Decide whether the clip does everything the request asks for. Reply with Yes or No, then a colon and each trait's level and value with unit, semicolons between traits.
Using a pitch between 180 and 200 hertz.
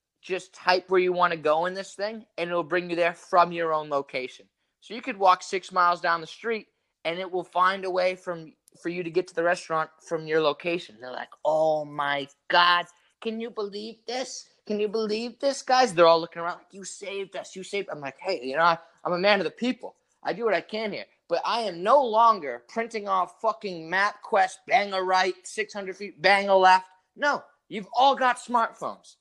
Yes: medium, 185 Hz